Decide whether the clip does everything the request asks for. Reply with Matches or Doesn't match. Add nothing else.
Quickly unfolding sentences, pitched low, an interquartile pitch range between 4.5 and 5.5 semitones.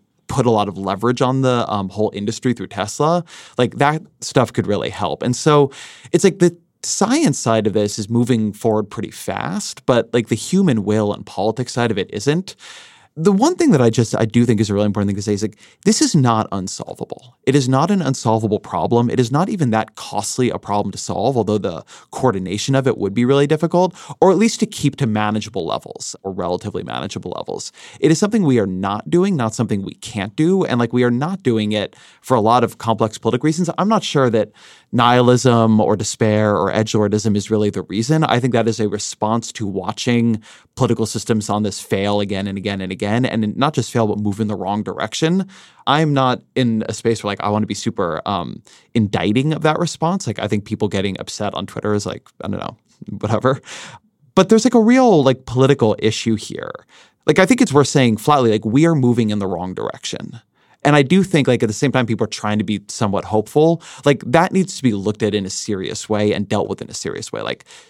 Matches